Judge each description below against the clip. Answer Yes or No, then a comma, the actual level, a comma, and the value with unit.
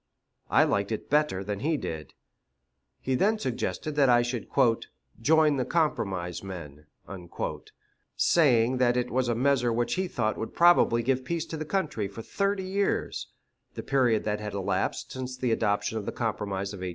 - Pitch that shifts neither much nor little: No, wide, 6.2 semitones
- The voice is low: Yes, low, 120 Hz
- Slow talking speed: No, average, 175 wpm